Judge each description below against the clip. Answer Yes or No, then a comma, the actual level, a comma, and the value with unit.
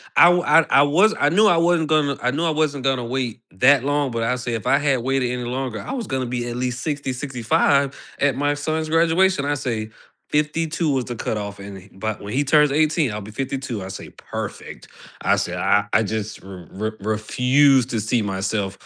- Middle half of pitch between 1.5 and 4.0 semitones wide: No, average, 4.8 semitones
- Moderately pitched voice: No, low, 130 Hz